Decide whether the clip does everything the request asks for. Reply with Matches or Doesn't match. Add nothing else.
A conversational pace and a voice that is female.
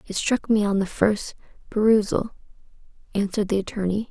Matches